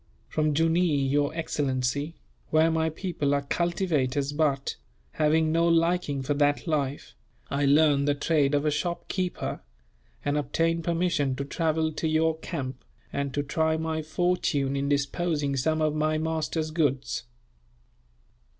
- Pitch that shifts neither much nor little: No, narrow, 2.3 semitones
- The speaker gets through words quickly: No, average, 140 wpm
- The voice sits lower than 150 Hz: No, medium, 155 Hz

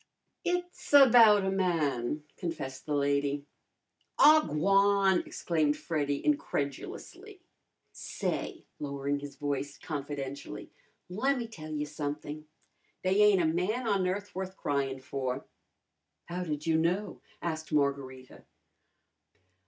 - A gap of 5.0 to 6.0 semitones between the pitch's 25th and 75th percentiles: Yes, wide, 5.4 semitones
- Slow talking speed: Yes, slow, 110 wpm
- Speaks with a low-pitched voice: No, medium, 155 Hz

